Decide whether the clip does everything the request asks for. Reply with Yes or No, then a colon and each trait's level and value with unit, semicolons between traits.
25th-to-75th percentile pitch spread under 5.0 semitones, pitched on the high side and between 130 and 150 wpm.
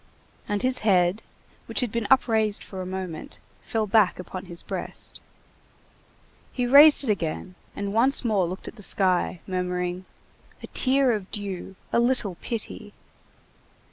Yes: average, 4.2 semitones; high, 205 Hz; average, 145 wpm